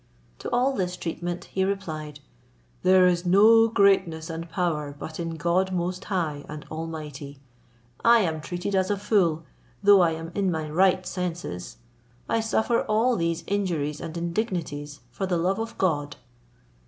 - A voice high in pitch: No, medium, 175 Hz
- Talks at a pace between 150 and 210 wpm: Yes, average, 155 wpm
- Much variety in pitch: No, average, 3.4 semitones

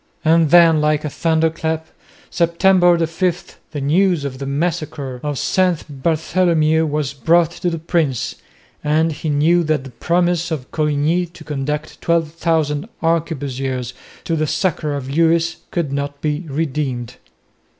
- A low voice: No, medium, 160 Hz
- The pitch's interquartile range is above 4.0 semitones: No, average, 2.7 semitones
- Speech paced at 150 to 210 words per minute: No, average, 140 wpm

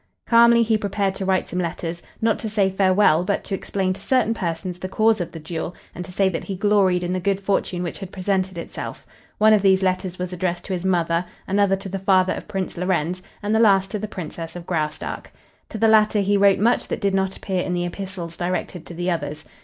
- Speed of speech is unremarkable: No, fast, 235 wpm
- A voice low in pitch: No, high, 190 Hz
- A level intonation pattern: Yes, narrow, 2.2 semitones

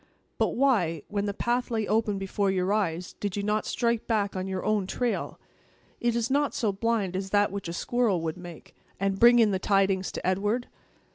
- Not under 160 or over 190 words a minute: No, fast, 205 wpm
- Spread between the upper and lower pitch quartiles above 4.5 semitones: No, average, 3.3 semitones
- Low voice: No, high, 205 Hz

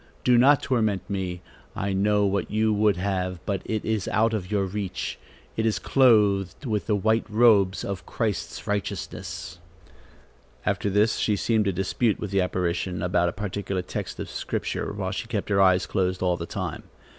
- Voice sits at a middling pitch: No, low, 100 Hz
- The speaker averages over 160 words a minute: Yes, average, 180 wpm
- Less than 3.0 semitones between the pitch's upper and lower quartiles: Yes, narrow, 2.6 semitones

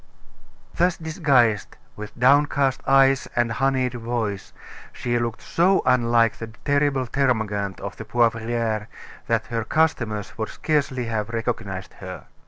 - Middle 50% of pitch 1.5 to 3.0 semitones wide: No, average, 3.6 semitones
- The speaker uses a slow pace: Yes, slow, 125 wpm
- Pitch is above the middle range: No, low, 120 Hz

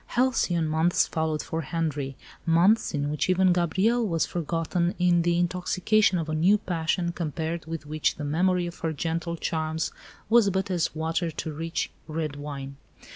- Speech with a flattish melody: Yes, narrow, 2.3 semitones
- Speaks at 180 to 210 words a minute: No, average, 165 wpm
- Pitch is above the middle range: No, medium, 165 Hz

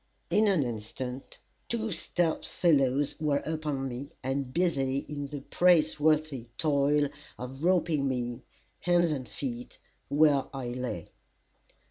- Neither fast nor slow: No, slow, 120 wpm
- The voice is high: No, medium, 140 Hz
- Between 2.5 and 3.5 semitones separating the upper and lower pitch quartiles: Yes, average, 3.2 semitones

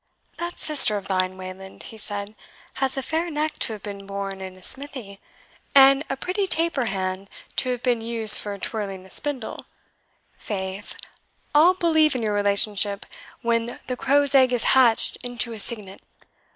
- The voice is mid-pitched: No, high, 230 Hz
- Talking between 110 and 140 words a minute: No, average, 165 wpm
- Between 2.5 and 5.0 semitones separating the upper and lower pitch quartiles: No, wide, 5.4 semitones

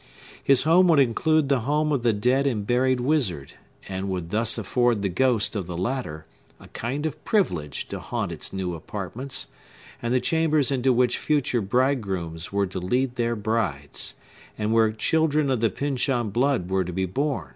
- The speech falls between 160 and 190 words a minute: Yes, average, 180 wpm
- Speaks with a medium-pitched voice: No, low, 120 Hz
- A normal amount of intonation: No, wide, 6.0 semitones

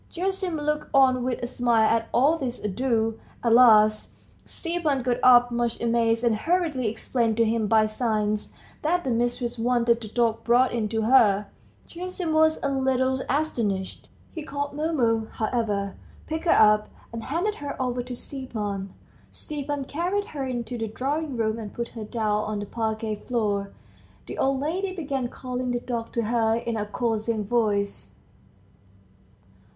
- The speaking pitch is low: No, high, 240 Hz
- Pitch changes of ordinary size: Yes, average, 3.7 semitones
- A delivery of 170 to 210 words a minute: No, average, 160 wpm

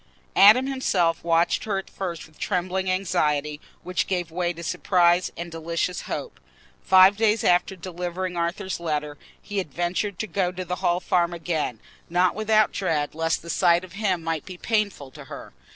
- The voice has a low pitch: No, medium, 180 Hz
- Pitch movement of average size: No, narrow, 2.2 semitones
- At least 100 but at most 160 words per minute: No, average, 170 wpm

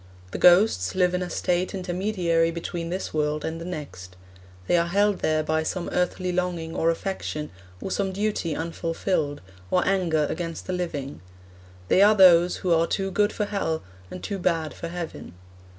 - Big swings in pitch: No, narrow, 2.4 semitones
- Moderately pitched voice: Yes, medium, 175 Hz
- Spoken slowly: No, average, 175 wpm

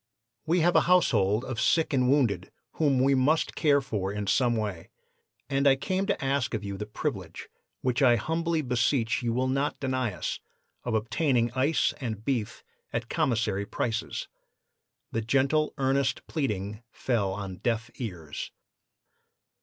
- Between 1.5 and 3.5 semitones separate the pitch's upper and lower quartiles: No, average, 4.2 semitones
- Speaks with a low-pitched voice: Yes, low, 125 Hz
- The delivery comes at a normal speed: Yes, average, 155 wpm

